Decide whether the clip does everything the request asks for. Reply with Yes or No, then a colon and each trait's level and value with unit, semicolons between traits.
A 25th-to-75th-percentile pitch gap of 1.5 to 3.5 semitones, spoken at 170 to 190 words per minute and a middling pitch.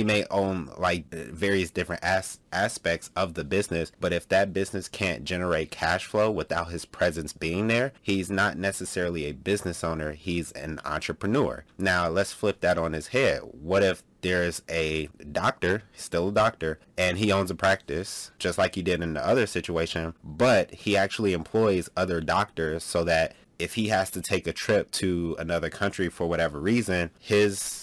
No: average, 2.9 semitones; average, 180 wpm; very low, 90 Hz